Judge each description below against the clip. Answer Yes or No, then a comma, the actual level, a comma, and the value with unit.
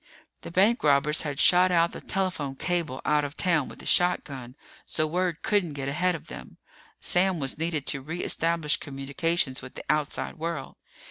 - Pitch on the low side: No, medium, 160 Hz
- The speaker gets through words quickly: No, average, 175 wpm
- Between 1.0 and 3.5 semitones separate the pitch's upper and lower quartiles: No, average, 4.0 semitones